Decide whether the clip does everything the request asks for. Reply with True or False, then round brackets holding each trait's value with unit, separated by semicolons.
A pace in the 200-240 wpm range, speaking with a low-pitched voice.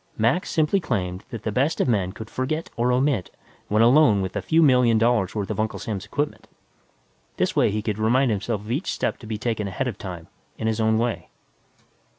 True (205 wpm; 115 Hz)